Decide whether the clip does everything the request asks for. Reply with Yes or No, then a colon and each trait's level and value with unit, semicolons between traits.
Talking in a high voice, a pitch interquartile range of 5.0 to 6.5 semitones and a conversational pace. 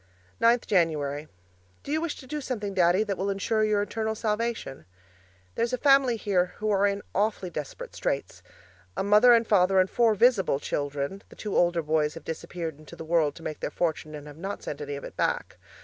No: high, 195 Hz; wide, 5.6 semitones; fast, 210 wpm